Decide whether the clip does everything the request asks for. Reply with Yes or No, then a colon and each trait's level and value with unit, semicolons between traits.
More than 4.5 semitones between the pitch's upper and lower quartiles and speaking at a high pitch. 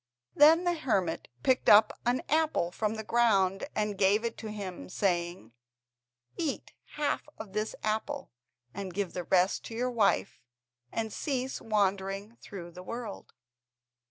No: average, 3.9 semitones; high, 210 Hz